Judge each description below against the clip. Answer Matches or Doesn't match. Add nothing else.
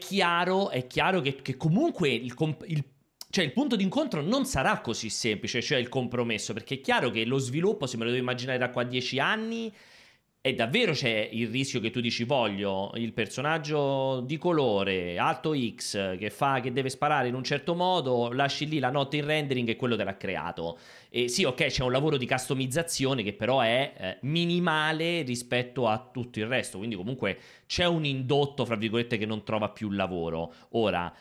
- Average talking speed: Doesn't match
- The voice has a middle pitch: Doesn't match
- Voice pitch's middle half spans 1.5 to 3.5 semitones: Doesn't match